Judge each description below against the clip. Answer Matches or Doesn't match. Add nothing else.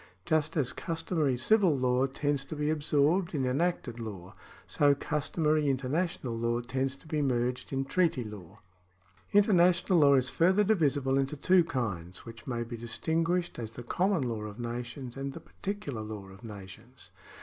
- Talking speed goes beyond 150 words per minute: Matches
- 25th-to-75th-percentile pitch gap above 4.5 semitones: Matches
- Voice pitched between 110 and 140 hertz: Matches